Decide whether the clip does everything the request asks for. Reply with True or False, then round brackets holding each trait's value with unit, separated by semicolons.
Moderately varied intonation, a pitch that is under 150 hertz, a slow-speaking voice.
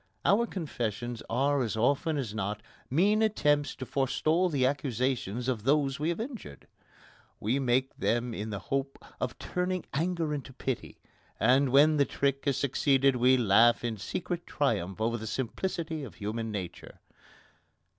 False (4.3 semitones; 135 Hz; 155 wpm)